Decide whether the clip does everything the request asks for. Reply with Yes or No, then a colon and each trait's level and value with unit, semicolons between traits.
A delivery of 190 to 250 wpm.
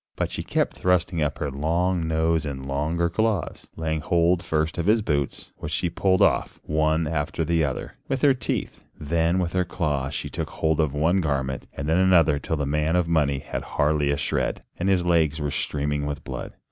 Yes: fast, 205 wpm